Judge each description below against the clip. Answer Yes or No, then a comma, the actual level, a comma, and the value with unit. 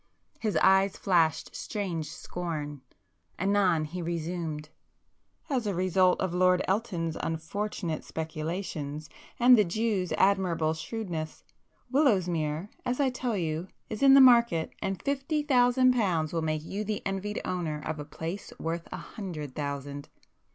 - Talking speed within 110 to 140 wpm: Yes, slow, 135 wpm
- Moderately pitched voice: Yes, medium, 180 Hz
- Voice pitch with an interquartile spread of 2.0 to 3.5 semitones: No, average, 4.8 semitones